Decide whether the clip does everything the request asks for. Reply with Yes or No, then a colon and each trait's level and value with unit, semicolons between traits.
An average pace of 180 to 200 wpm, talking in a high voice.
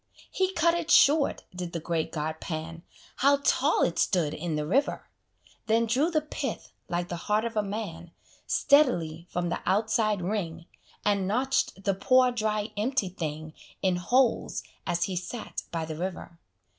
No: average, 165 wpm; high, 195 Hz